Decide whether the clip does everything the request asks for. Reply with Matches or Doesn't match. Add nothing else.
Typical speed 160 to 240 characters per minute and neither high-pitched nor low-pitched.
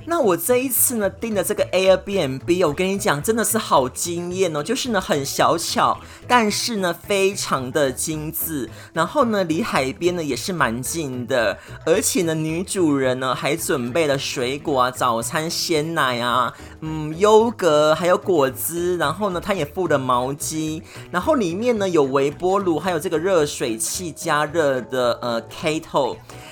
Doesn't match